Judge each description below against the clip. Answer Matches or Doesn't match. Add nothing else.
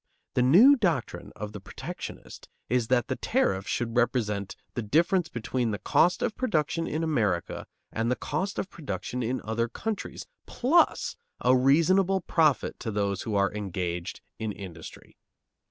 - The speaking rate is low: Doesn't match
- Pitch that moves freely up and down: Matches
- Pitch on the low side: Matches